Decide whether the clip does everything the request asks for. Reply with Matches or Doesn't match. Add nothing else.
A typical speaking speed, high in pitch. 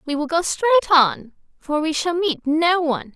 Doesn't match